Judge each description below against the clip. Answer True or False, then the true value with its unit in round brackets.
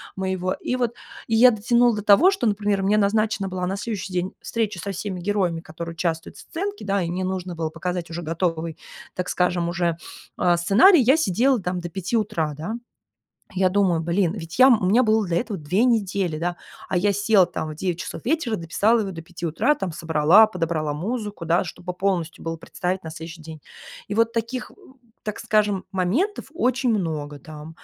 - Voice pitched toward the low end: False (185 Hz)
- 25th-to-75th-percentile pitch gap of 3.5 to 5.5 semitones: True (4.3 semitones)